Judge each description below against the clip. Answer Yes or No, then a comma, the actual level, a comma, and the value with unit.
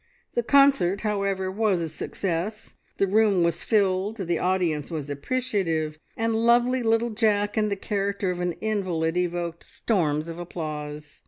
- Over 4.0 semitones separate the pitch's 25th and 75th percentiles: Yes, average, 4.4 semitones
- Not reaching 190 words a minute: Yes, average, 150 wpm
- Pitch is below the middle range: No, high, 190 Hz